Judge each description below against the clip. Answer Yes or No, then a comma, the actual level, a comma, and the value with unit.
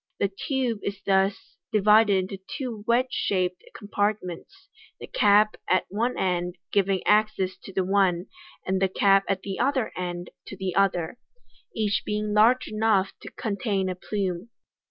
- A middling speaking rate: Yes, average, 160 wpm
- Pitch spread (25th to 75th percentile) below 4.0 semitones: Yes, narrow, 2.4 semitones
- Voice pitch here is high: Yes, high, 200 Hz